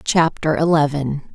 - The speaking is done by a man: No, female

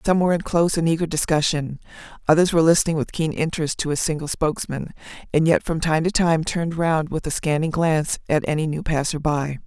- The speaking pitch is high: No, medium, 160 Hz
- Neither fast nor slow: No, fast, 210 wpm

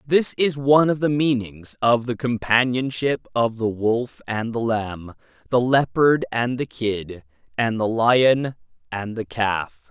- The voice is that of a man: Yes, male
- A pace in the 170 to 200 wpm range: No, average, 155 wpm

